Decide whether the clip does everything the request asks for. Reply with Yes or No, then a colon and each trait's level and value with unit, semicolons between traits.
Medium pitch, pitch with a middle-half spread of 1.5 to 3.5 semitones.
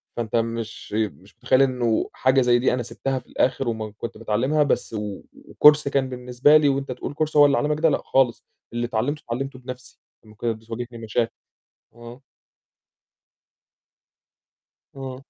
No: low, 125 Hz; average, 2.9 semitones